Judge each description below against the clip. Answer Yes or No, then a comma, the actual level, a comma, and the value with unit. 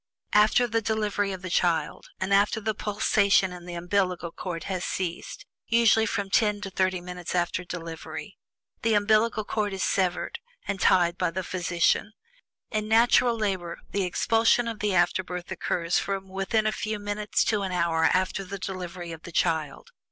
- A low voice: No, high, 190 Hz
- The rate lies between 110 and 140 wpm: No, average, 170 wpm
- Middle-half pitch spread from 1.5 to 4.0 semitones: Yes, average, 3.1 semitones